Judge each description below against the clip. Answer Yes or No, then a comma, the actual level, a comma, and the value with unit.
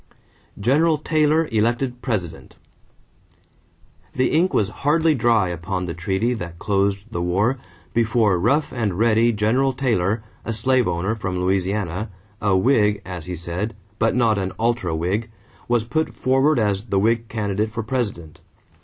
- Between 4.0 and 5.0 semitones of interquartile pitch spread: Yes, average, 4.3 semitones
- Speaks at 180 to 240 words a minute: No, average, 145 wpm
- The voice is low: Yes, low, 110 Hz